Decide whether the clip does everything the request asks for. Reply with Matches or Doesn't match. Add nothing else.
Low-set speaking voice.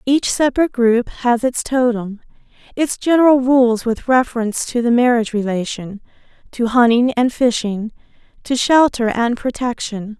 Doesn't match